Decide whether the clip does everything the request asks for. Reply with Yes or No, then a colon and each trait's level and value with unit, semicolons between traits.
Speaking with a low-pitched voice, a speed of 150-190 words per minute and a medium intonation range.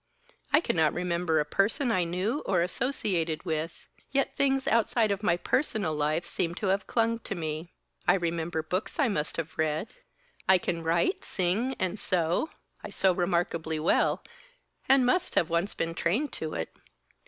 No: medium, 175 Hz; average, 165 wpm; average, 5.0 semitones